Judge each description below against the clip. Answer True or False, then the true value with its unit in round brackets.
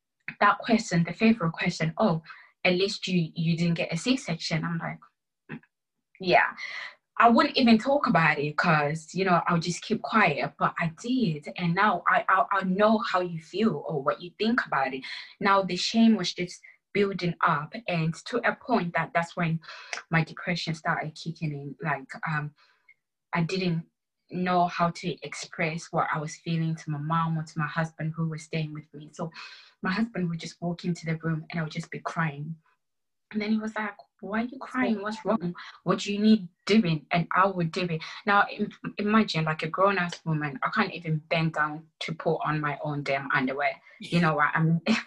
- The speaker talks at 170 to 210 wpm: True (200 wpm)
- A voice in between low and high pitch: True (170 Hz)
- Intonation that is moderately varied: True (3.7 semitones)